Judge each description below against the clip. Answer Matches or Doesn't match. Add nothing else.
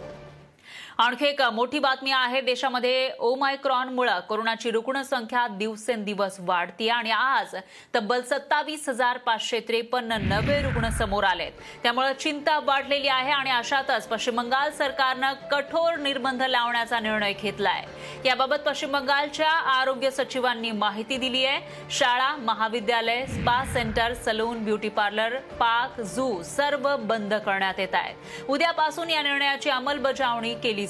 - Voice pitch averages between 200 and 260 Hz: Matches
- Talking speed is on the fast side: Doesn't match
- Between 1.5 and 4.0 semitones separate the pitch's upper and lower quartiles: Matches